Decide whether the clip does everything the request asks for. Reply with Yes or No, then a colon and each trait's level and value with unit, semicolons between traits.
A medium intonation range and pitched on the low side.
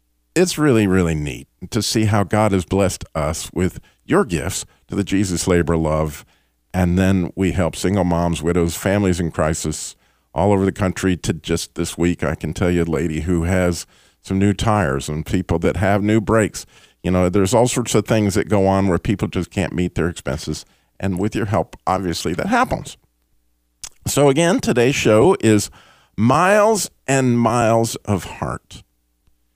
Yes: average, 4.3 semitones; very low, 95 Hz